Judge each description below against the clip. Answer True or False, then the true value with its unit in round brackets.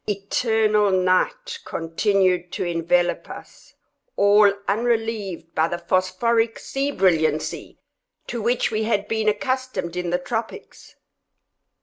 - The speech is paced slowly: True (110 wpm)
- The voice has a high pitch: True (205 Hz)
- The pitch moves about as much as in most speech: True (4.1 semitones)